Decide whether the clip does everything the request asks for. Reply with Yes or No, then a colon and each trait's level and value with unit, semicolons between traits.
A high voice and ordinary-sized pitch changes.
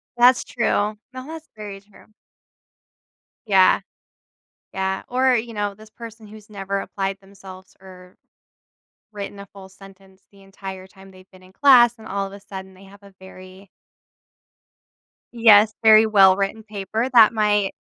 No: high, 200 Hz; narrow, 2.2 semitones